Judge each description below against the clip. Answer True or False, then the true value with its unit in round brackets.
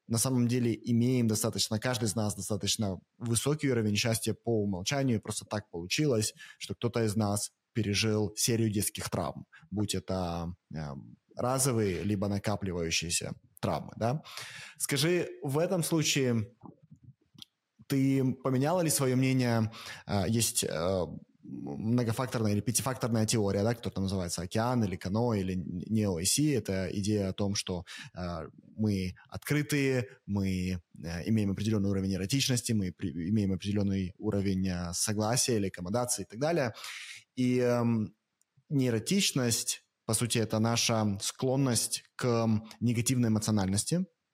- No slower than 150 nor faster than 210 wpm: False (130 wpm)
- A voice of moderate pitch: False (110 Hz)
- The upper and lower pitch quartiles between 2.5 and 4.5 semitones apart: True (3.9 semitones)